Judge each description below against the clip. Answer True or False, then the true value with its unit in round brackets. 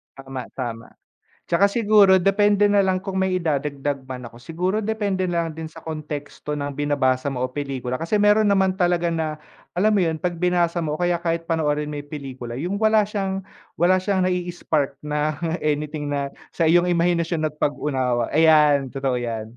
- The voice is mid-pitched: True (160 Hz)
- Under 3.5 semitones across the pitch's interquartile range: False (4.5 semitones)